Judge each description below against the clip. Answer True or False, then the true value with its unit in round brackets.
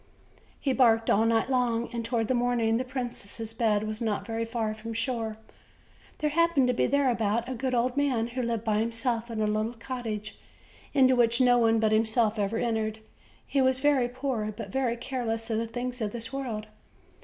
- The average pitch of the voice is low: False (230 Hz)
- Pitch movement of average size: False (2.2 semitones)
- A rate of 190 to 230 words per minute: True (200 wpm)